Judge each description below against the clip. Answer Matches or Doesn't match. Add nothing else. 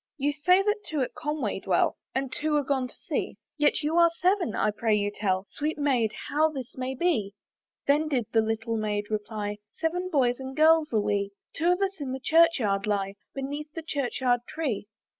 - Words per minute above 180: Matches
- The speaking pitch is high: Matches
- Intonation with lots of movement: Matches